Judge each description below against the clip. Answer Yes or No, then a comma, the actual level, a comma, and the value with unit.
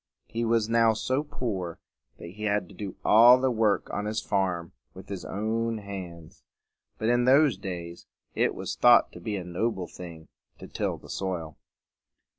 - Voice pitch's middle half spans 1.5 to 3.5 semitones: No, average, 4.2 semitones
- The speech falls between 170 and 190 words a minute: Yes, average, 175 wpm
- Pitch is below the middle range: Yes, low, 105 Hz